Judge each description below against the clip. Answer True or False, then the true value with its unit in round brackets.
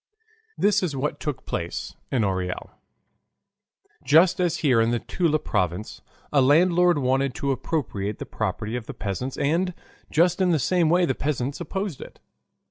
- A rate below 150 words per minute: False (160 wpm)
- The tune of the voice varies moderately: False (6.1 semitones)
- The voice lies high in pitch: False (140 Hz)